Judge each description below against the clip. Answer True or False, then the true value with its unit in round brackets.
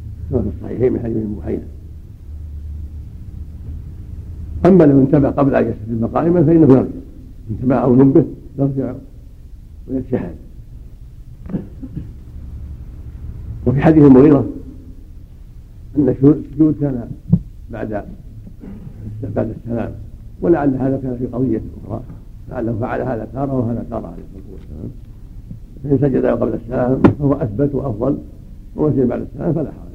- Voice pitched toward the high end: False (115 Hz)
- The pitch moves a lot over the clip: True (7.4 semitones)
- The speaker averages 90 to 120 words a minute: True (110 wpm)